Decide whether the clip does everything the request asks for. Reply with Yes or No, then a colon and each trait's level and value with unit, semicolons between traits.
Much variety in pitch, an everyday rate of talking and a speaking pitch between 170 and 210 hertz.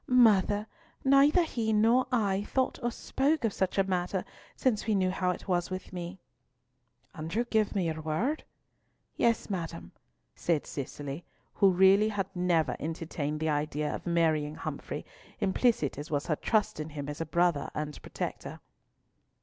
Yes: wide, 5.7 semitones; average, 165 wpm; medium, 185 Hz